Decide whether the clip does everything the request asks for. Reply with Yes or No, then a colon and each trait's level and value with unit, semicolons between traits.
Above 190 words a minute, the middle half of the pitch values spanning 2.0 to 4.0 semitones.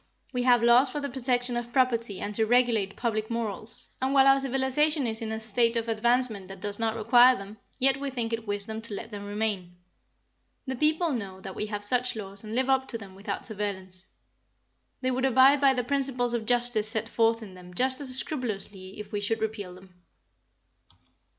Yes: average, 200 wpm; average, 3.6 semitones